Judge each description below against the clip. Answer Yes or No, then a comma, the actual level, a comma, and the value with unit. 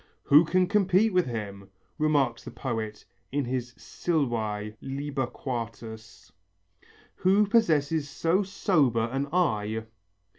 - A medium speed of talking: No, slow, 110 wpm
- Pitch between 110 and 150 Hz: Yes, low, 135 Hz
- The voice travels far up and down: Yes, wide, 6.9 semitones